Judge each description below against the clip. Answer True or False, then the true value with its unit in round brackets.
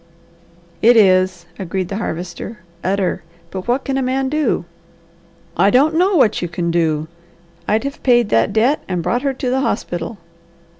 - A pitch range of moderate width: False (6.7 semitones)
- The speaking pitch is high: True (215 Hz)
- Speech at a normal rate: True (165 wpm)